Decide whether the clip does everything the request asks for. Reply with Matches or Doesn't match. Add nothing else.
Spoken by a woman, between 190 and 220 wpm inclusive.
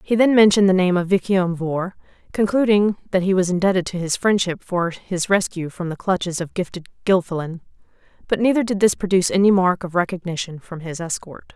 Matches